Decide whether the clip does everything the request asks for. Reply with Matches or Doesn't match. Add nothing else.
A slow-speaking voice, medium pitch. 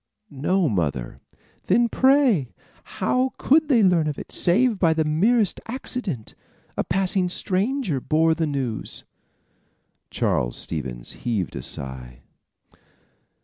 Matches